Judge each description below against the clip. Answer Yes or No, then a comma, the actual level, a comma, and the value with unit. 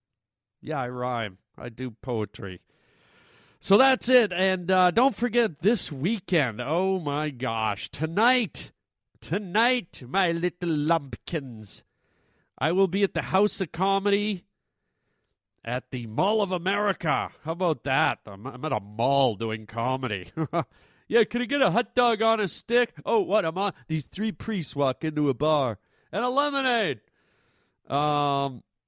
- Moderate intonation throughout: No, wide, 8.3 semitones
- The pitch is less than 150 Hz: No, medium, 160 Hz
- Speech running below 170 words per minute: Yes, average, 150 wpm